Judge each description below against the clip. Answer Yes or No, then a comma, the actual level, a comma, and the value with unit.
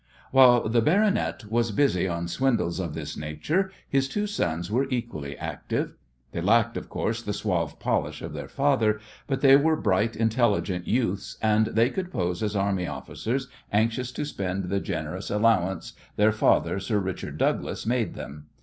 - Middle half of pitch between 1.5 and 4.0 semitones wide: No, wide, 5.4 semitones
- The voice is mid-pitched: No, low, 110 Hz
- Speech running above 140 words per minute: Yes, average, 165 wpm